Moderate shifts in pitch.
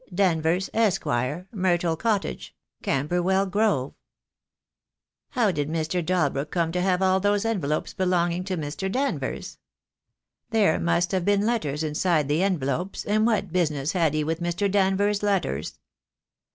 Yes: average, 3.9 semitones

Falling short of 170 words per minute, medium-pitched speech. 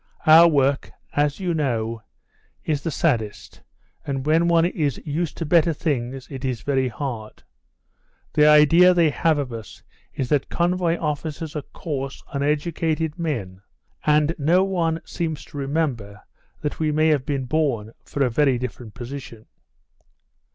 Yes: average, 150 wpm; medium, 150 Hz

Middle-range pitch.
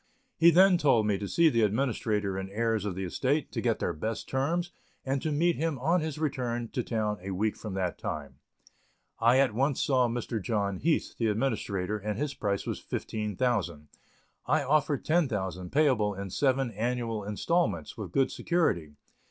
No: low, 115 Hz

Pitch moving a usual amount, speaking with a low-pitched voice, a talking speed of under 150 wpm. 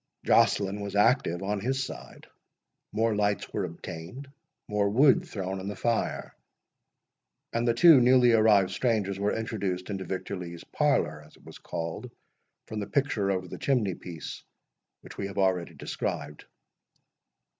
Yes: average, 3.7 semitones; low, 100 Hz; average, 140 wpm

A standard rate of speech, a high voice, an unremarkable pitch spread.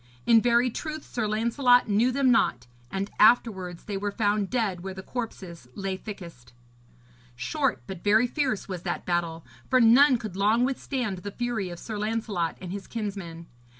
Yes: average, 170 wpm; high, 210 Hz; average, 4.3 semitones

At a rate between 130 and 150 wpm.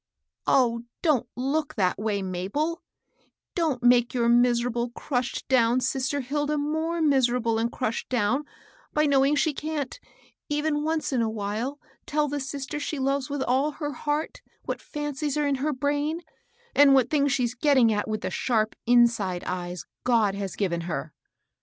No: average, 165 wpm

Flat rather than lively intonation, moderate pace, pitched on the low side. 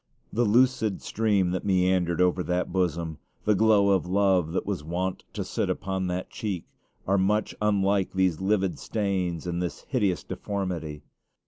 Yes: narrow, 2.3 semitones; average, 155 wpm; very low, 95 Hz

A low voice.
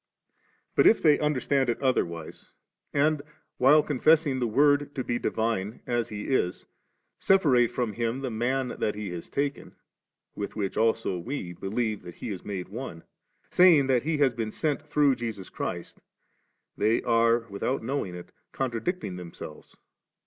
Yes: low, 120 Hz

